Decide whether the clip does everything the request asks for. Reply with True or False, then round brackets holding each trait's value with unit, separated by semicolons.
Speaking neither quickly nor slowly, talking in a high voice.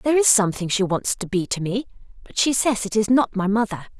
False (255 wpm; 215 Hz)